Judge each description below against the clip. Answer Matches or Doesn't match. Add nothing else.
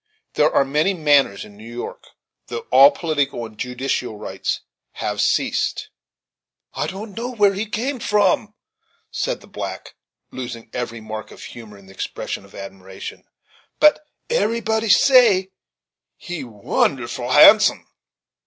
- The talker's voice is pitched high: Doesn't match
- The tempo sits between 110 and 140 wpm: Matches